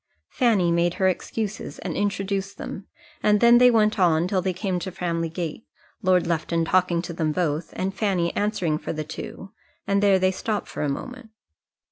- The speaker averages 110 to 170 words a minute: No, average, 185 wpm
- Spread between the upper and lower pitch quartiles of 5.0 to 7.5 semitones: No, average, 3.2 semitones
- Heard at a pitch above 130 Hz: Yes, medium, 185 Hz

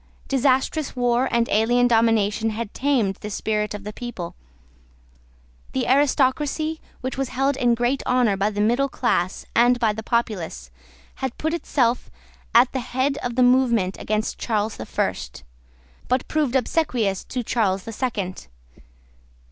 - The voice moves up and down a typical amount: Yes, average, 3.7 semitones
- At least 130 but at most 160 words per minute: Yes, average, 150 wpm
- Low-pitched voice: No, high, 240 Hz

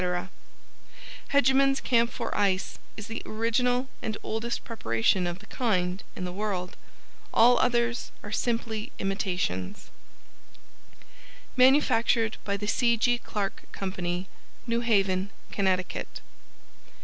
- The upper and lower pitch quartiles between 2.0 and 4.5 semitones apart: Yes, average, 4.0 semitones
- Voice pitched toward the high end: Yes, high, 215 Hz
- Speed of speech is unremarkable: No, slow, 105 wpm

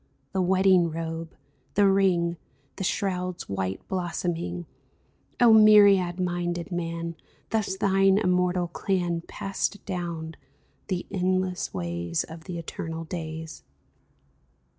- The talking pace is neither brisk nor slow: No, slow, 105 wpm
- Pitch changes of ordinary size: No, narrow, 2.3 semitones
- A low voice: No, medium, 175 Hz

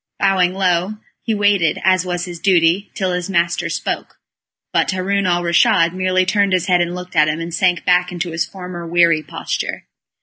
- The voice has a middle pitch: Yes, medium, 180 Hz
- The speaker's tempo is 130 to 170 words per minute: No, average, 190 wpm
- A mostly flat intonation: Yes, narrow, 1.6 semitones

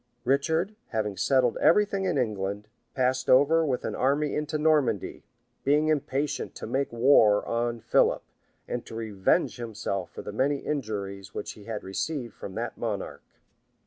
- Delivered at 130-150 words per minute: No, average, 160 wpm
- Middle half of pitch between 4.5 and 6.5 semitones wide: Yes, wide, 5.4 semitones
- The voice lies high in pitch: No, low, 125 Hz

